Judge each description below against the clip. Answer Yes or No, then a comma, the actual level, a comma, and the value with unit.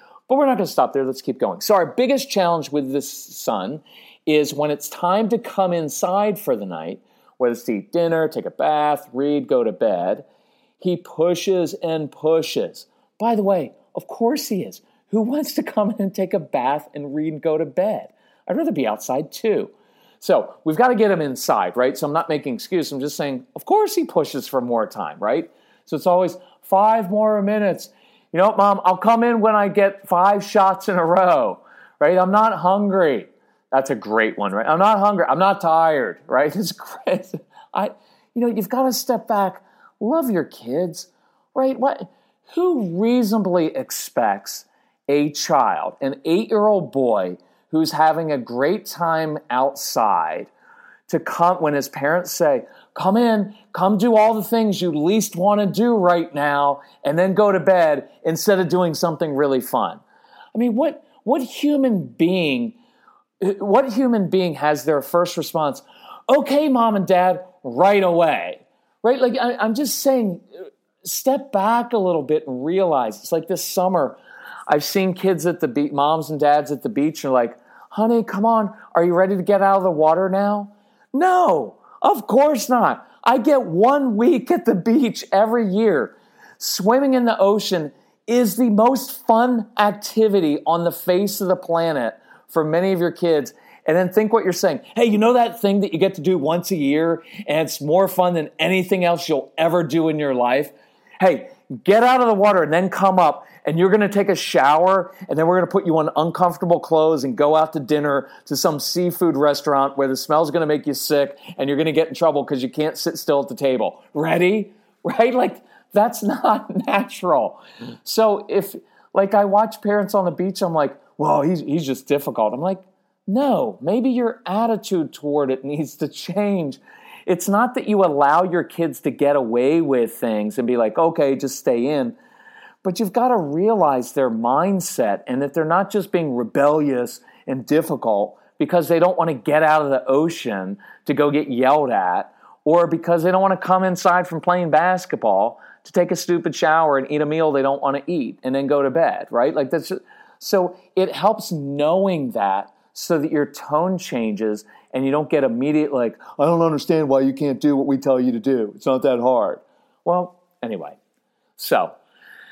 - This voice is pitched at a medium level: Yes, medium, 180 Hz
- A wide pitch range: Yes, wide, 5.9 semitones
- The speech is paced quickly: No, average, 195 wpm